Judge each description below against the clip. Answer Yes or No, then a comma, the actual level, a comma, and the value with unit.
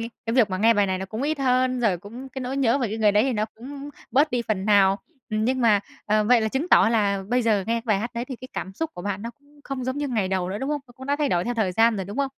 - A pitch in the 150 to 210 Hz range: No, high, 230 Hz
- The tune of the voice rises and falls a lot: No, average, 4.1 semitones